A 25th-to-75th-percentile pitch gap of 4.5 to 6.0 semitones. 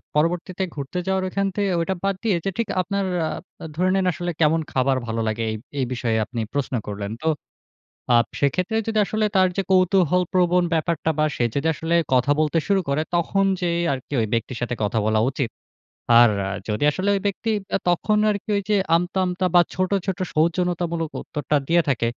Yes: average, 5.3 semitones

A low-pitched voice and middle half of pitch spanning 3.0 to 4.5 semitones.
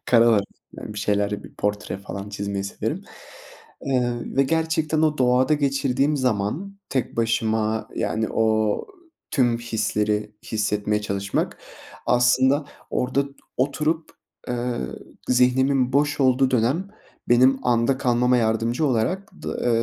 Yes: low, 125 Hz; average, 3.8 semitones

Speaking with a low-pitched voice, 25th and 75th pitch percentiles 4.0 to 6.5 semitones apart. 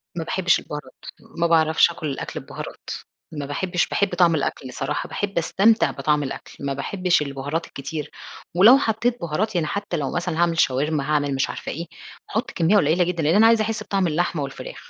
No: medium, 170 Hz; average, 4.6 semitones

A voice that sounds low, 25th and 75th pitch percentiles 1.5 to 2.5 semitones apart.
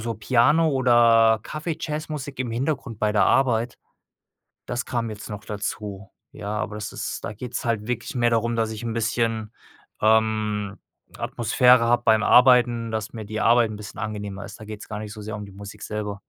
Yes: low, 110 Hz; narrow, 2.2 semitones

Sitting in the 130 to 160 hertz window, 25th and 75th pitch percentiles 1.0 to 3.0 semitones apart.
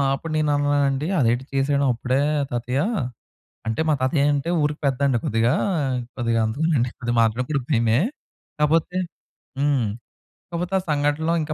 No: medium, 140 Hz; average, 3.6 semitones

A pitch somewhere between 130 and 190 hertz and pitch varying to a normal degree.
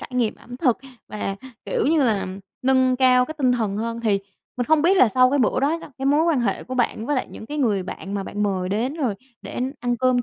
No: very high, 250 Hz; average, 3.8 semitones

